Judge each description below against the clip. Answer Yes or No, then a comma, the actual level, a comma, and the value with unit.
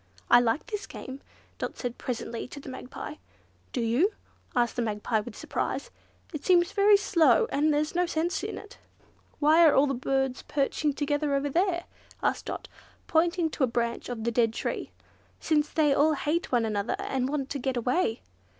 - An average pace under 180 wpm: No, average, 190 wpm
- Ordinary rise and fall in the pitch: Yes, average, 4.7 semitones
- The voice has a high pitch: Yes, very high, 280 Hz